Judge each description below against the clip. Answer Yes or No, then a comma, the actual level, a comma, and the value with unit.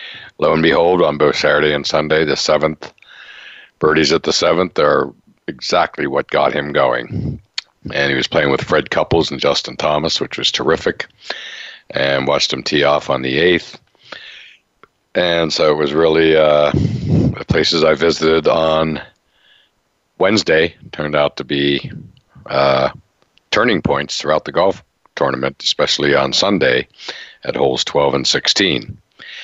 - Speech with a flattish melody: Yes, narrow, 2.0 semitones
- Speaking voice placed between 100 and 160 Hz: No, very low, 75 Hz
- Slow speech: No, average, 145 wpm